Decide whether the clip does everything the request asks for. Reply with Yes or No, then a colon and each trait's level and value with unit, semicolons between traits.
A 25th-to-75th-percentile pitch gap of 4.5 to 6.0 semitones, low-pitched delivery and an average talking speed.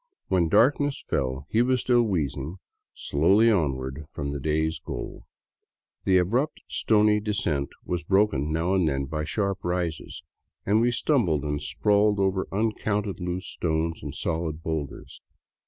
Yes: wide, 5.4 semitones; very low, 90 Hz; average, 150 wpm